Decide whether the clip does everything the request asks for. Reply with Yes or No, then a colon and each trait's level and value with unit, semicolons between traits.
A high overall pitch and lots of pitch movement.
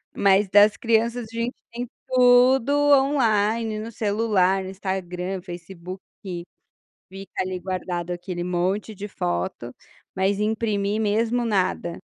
No: high, 200 Hz; average, 3.8 semitones